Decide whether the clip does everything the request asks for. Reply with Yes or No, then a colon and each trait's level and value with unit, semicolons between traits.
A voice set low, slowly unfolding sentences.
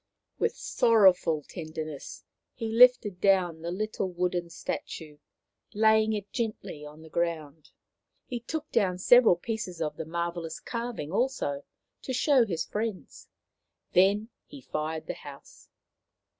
No: medium, 185 Hz; slow, 130 wpm